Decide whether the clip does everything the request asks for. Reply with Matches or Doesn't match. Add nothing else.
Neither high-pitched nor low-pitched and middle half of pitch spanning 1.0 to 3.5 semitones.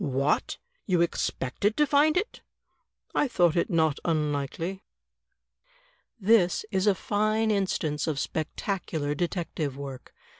Doesn't match